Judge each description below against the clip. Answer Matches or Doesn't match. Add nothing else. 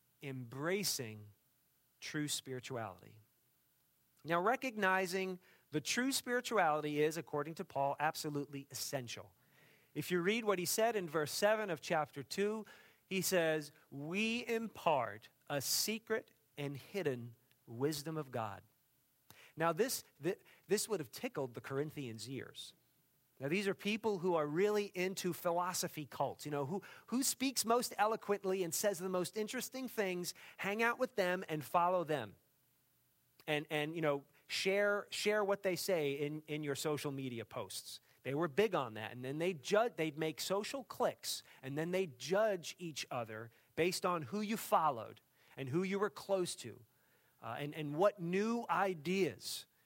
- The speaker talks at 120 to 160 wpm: Matches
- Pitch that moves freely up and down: Matches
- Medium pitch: Matches